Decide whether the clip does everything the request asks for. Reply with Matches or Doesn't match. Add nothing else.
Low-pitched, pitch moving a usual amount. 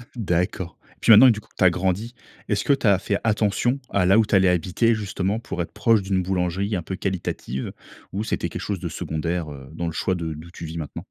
Matches